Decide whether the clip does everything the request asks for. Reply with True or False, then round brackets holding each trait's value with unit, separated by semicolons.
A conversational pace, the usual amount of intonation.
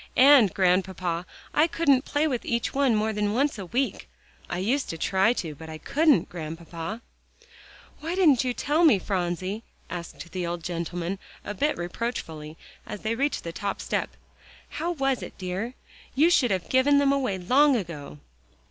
False (170 wpm; 7.6 semitones)